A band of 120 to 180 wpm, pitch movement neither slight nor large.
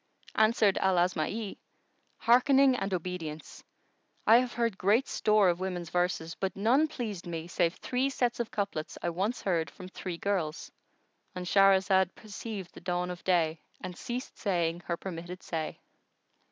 Yes: average, 150 wpm; average, 3.9 semitones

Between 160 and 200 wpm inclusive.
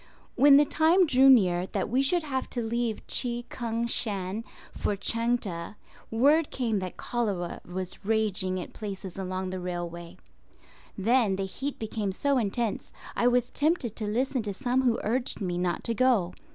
Yes: average, 170 wpm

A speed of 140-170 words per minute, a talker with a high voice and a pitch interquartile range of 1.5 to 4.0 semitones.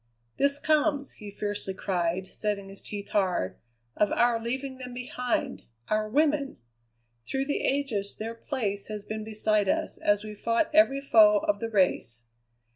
No: average, 155 wpm; high, 215 Hz; average, 4.7 semitones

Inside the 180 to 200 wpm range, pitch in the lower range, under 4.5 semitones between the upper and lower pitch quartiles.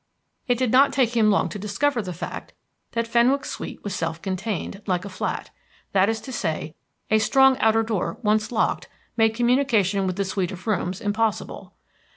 No: average, 185 wpm; high, 215 Hz; average, 3.6 semitones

